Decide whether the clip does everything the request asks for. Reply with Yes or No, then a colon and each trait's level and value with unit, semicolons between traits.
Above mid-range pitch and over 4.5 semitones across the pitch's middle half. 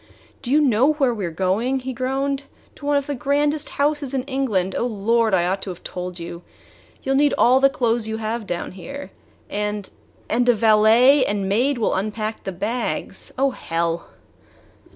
Yes: high, 235 Hz; average, 5.1 semitones